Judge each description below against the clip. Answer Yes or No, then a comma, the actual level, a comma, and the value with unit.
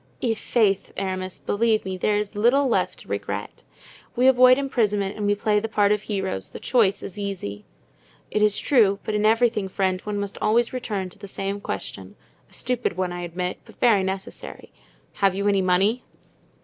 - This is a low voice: No, high, 205 Hz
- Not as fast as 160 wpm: No, average, 175 wpm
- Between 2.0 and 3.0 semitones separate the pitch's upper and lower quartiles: Yes, average, 2.7 semitones